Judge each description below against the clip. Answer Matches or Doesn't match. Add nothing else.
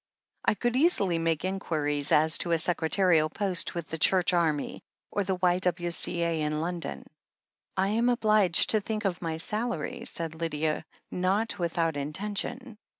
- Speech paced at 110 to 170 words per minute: Matches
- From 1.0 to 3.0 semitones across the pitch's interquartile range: Doesn't match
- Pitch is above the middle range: Doesn't match